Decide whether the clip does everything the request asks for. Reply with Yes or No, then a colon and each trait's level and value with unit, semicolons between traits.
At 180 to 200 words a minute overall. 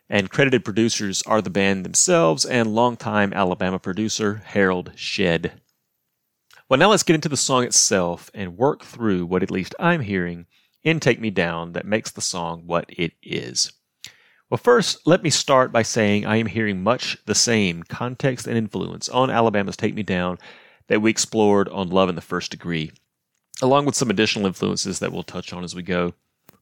Yes: average, 185 wpm